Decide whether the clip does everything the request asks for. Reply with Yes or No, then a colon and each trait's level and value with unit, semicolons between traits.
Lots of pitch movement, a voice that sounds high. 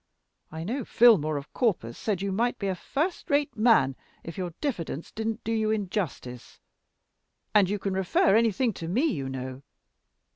Yes: wide, 5.8 semitones; high, 200 Hz